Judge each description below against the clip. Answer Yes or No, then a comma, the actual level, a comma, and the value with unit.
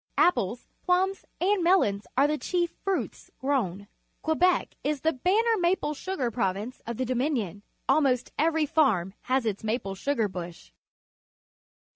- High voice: Yes, very high, 270 Hz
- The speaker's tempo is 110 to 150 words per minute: Yes, average, 140 wpm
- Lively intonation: Yes, wide, 8.1 semitones